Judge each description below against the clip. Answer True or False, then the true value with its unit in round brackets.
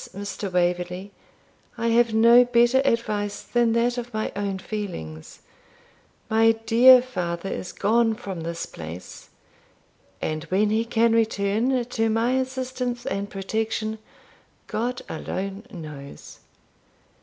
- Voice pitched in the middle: False (220 Hz)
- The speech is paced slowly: True (120 wpm)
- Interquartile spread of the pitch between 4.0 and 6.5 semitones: False (3.6 semitones)